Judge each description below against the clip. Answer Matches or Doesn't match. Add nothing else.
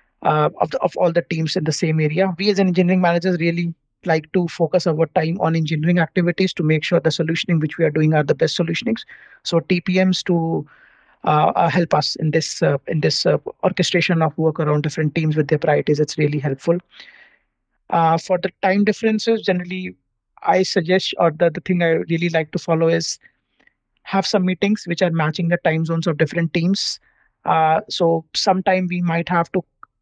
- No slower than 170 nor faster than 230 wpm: Matches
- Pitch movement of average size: Doesn't match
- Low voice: Doesn't match